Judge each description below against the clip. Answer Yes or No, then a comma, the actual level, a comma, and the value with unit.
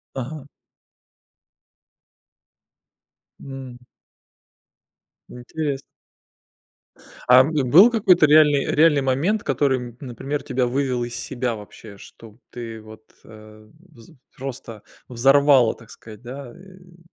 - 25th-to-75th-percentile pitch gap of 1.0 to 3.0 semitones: No, average, 3.8 semitones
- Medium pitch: No, low, 130 Hz